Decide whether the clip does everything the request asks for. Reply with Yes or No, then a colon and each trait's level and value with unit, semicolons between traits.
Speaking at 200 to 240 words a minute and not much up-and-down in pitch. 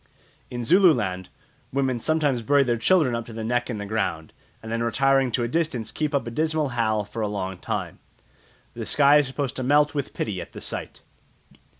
No: fast, 205 wpm; average, 4.3 semitones